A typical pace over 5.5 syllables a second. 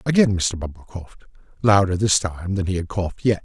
Yes: 5.9 syllables/s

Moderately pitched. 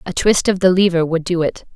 Yes: medium, 175 Hz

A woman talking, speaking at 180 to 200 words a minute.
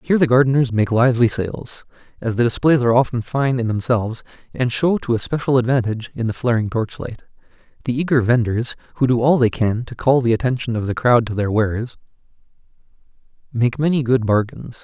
No: male; average, 185 wpm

